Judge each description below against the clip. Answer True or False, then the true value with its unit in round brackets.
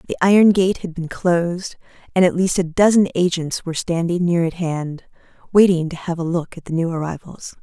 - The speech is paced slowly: False (205 wpm)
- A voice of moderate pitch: True (175 Hz)